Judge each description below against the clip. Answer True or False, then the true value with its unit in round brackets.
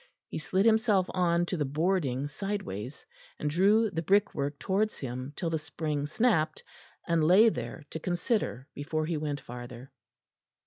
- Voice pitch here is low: False (160 Hz)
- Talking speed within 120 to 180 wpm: True (150 wpm)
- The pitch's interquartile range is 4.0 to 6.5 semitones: True (5.1 semitones)